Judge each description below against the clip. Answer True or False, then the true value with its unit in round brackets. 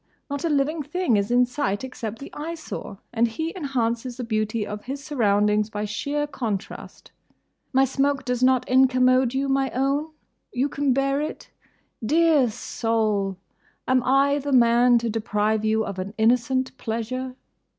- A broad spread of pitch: False (3.7 semitones)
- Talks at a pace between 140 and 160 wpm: True (150 wpm)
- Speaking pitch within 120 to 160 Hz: False (250 Hz)